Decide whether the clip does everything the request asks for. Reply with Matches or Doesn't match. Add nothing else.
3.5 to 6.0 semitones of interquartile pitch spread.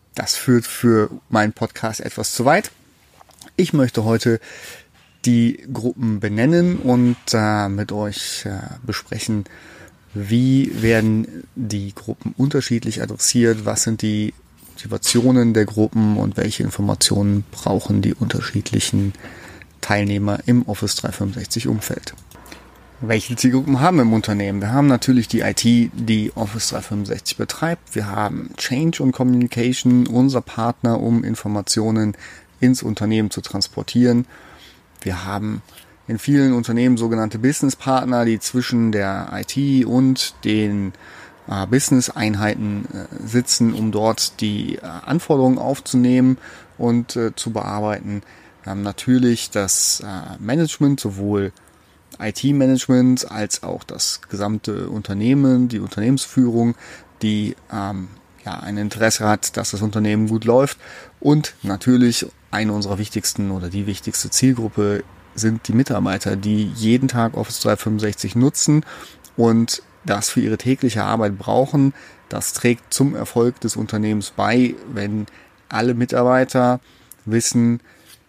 Doesn't match